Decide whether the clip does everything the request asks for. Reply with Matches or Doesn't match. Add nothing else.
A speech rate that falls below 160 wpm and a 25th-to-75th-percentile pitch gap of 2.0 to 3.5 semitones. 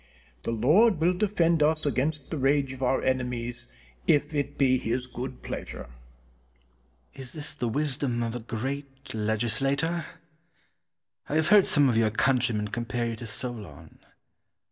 Doesn't match